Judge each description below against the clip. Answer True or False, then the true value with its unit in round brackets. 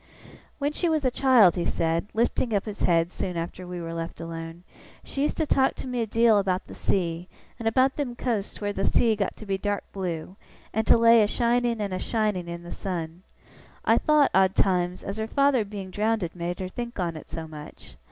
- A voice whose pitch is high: True (200 Hz)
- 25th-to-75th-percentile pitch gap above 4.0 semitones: True (5.0 semitones)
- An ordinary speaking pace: False (220 wpm)